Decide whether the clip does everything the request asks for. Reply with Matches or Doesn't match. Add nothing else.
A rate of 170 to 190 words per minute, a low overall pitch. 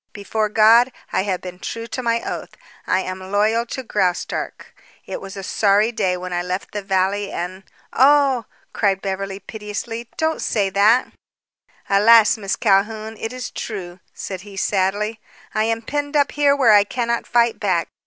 Doesn't match